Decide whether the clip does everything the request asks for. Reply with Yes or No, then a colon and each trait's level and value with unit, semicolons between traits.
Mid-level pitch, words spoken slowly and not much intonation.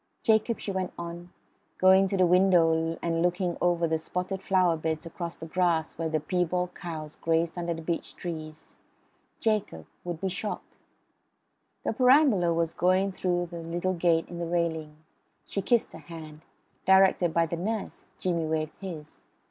No: medium, 175 Hz; average, 160 wpm; narrow, 2.3 semitones